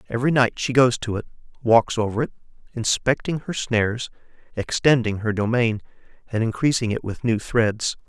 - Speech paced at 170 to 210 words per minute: No, average, 155 wpm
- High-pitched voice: No, low, 120 Hz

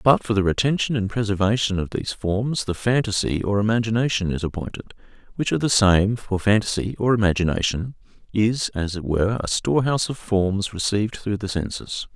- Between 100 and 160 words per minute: No, average, 175 wpm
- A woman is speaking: No, male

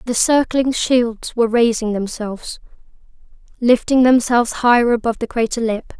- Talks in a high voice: Yes, high, 235 Hz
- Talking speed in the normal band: No, slow, 130 wpm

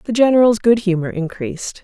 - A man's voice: No, female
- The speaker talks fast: No, average, 165 wpm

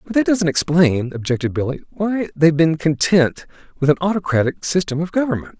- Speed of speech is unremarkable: Yes, average, 170 wpm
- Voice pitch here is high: No, medium, 165 Hz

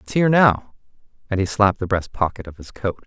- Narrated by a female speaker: No, male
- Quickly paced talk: Yes, fast, 235 wpm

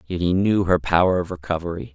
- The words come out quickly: Yes, fast, 215 wpm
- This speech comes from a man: Yes, male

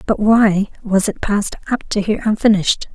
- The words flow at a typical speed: Yes, average, 185 wpm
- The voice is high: Yes, high, 205 Hz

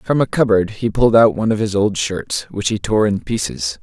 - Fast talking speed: Yes, fast, 250 wpm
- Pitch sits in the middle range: No, low, 105 Hz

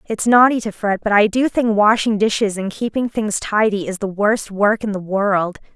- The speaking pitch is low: No, high, 210 Hz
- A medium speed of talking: No, fast, 220 wpm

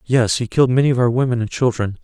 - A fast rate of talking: Yes, fast, 265 wpm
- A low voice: Yes, low, 120 Hz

